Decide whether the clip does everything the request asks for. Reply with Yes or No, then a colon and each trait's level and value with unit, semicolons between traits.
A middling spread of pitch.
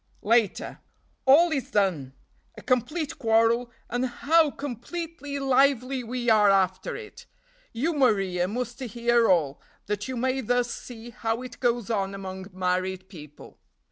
Yes: average, 4.9 semitones